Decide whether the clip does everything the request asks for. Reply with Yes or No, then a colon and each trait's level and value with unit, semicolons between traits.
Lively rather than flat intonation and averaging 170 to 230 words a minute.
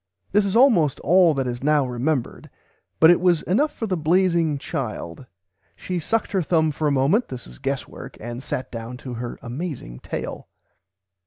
Yes: wide, 6.3 semitones; average, 175 wpm